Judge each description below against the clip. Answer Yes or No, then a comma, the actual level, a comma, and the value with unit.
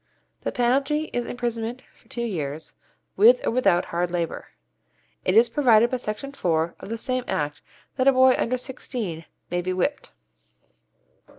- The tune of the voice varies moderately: No, wide, 6.4 semitones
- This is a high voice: Yes, high, 235 Hz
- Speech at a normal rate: Yes, average, 160 wpm